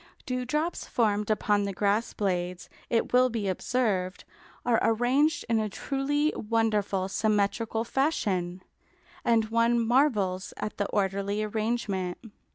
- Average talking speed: No, slow, 120 wpm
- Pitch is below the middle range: No, high, 220 Hz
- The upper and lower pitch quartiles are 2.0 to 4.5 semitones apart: Yes, average, 3.4 semitones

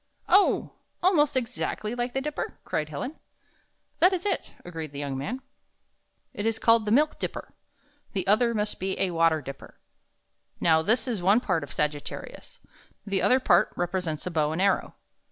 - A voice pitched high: Yes, high, 200 Hz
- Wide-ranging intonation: Yes, wide, 7.4 semitones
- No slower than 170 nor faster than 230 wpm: Yes, average, 185 wpm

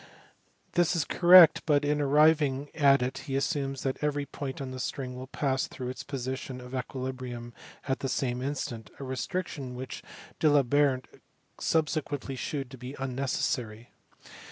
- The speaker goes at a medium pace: Yes, average, 155 wpm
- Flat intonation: Yes, narrow, 2.2 semitones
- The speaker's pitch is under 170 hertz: Yes, low, 135 Hz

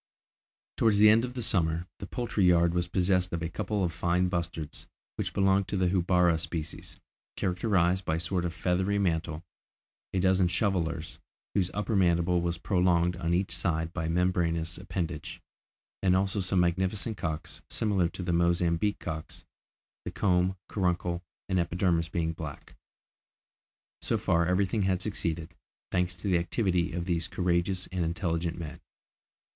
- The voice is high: No, very low, 90 Hz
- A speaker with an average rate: Yes, average, 155 wpm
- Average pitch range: No, narrow, 1.9 semitones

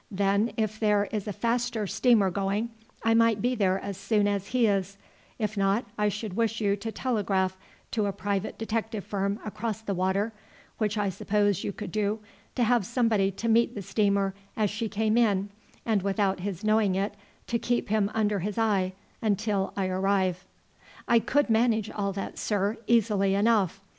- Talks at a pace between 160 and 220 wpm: Yes, average, 180 wpm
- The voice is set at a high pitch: Yes, high, 205 Hz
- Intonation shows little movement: Yes, narrow, 2.2 semitones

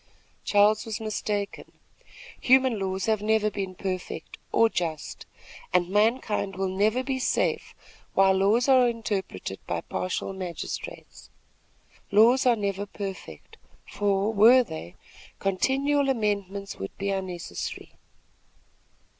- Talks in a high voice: Yes, high, 205 Hz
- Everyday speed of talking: No, slow, 115 wpm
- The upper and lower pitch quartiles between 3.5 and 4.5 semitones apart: No, average, 3.0 semitones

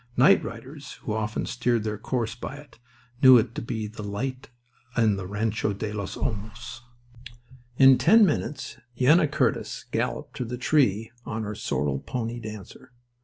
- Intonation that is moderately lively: Yes, average, 3.4 semitones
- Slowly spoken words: No, average, 160 wpm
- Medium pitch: No, low, 115 Hz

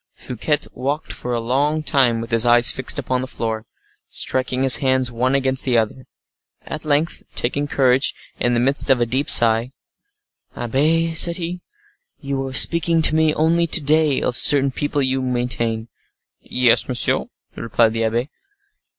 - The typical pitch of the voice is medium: No, low, 130 Hz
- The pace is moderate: Yes, average, 165 wpm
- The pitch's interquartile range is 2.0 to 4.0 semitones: Yes, average, 3.4 semitones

